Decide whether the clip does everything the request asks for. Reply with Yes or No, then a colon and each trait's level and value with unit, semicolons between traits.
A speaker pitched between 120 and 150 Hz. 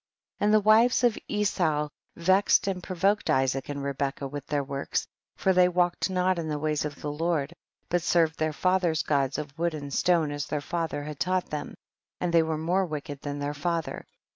No: medium, 160 Hz